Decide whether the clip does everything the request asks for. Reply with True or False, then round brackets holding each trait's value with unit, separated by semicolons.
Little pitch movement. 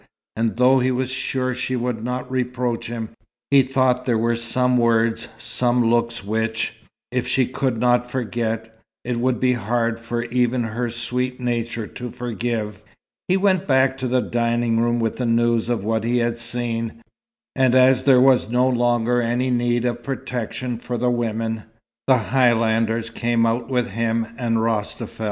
True (1.6 semitones)